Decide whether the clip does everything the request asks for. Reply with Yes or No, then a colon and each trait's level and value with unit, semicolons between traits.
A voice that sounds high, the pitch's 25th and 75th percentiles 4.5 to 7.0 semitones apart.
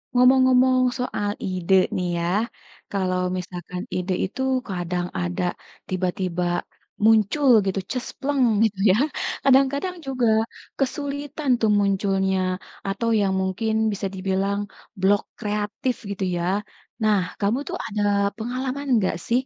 Yes: high, 205 Hz; average, 5.2 semitones